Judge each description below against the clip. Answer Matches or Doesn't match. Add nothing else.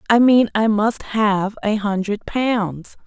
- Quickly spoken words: Doesn't match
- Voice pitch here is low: Doesn't match